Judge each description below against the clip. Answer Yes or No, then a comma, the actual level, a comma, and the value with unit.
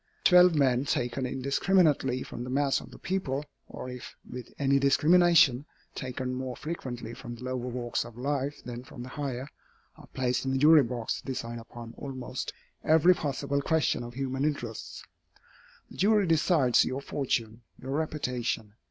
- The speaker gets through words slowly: No, average, 160 wpm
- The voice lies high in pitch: No, low, 130 Hz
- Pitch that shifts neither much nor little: Yes, average, 3.0 semitones